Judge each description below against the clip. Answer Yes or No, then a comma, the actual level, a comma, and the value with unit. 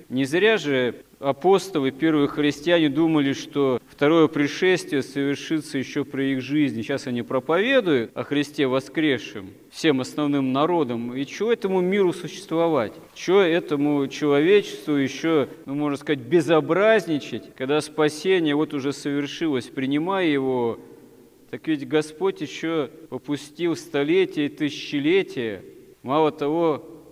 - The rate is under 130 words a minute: Yes, average, 120 wpm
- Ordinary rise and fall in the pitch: Yes, average, 3.4 semitones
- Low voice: No, medium, 150 Hz